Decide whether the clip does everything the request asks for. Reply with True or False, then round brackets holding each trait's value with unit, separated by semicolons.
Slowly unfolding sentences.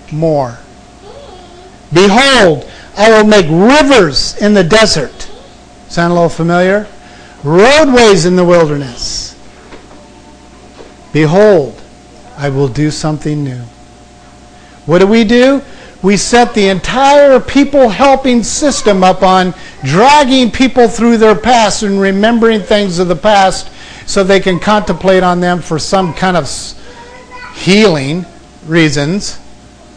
True (120 wpm)